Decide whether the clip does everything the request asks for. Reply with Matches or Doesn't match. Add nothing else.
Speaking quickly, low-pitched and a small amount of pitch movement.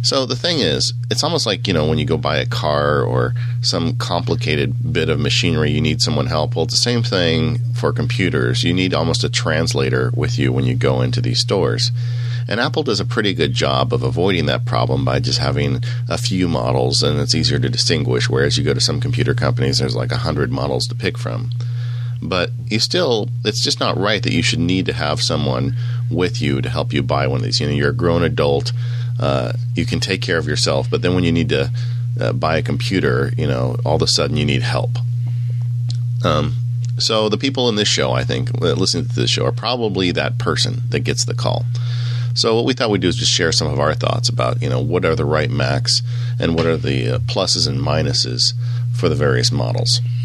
Matches